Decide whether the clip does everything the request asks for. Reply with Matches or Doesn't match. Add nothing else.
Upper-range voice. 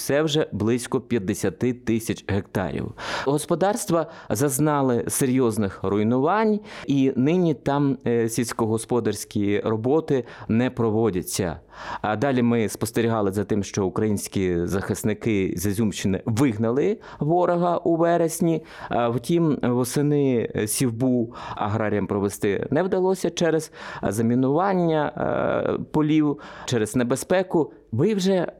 Doesn't match